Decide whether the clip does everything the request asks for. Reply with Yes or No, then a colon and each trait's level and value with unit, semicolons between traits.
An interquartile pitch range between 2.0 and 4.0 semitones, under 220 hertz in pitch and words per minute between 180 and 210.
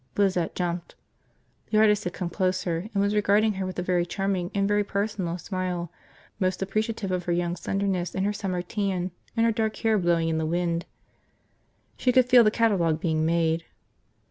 Yes: average, 3.0 semitones; medium, 185 Hz; average, 185 wpm